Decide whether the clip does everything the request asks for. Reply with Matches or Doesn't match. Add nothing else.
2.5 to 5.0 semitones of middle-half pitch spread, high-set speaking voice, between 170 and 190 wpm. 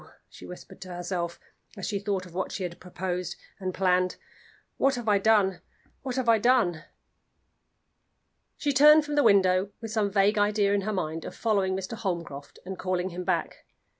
Matches